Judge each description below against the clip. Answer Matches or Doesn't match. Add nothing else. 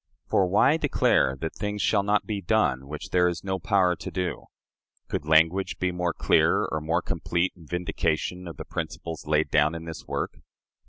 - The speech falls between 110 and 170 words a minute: Doesn't match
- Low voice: Matches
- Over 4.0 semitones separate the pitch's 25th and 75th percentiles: Doesn't match